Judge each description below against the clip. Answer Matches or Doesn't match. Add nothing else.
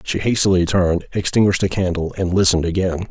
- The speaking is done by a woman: Doesn't match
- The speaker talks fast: Doesn't match